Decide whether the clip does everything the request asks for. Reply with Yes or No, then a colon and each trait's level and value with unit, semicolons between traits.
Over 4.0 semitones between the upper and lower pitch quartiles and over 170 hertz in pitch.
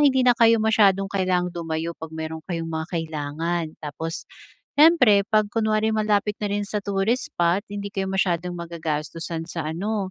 Yes: average, 4.4 semitones; medium, 185 Hz